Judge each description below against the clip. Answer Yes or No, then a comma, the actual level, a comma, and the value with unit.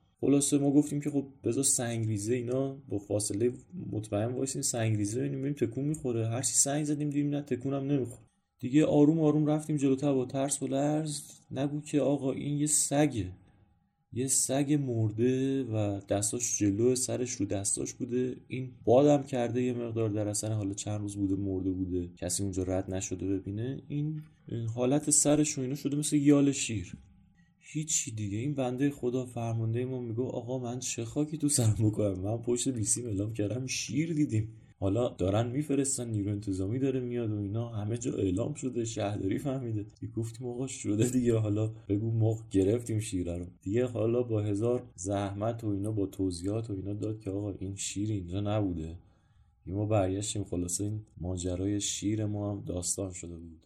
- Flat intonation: No, average, 5.0 semitones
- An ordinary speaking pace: No, fast, 175 wpm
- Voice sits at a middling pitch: No, low, 115 Hz